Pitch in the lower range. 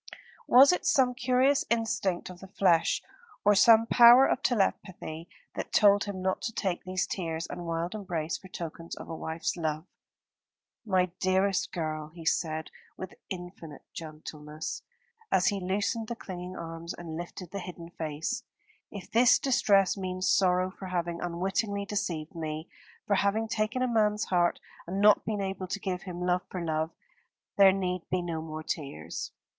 No: medium, 185 Hz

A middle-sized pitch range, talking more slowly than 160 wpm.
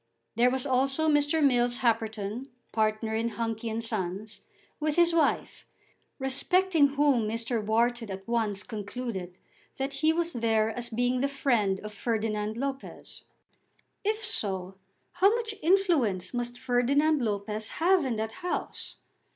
Yes: average, 4.6 semitones; slow, 135 wpm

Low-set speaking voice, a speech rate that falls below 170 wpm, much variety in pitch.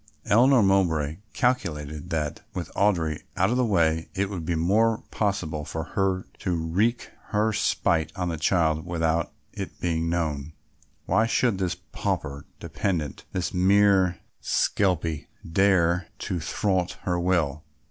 No: very low, 90 Hz; slow, 135 wpm; average, 3.6 semitones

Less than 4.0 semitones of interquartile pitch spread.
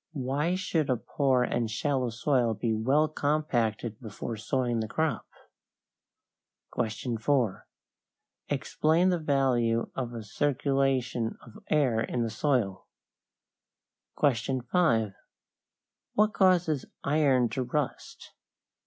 No: average, 4.3 semitones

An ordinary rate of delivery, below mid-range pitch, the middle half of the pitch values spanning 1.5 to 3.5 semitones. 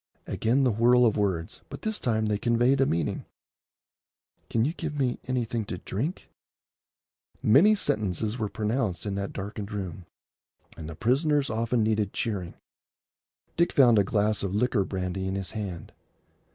No: average, 155 wpm; low, 110 Hz; average, 4.0 semitones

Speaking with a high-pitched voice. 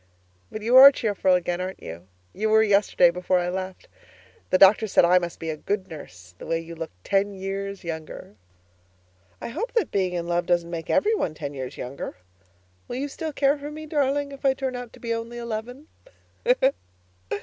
Yes: high, 195 Hz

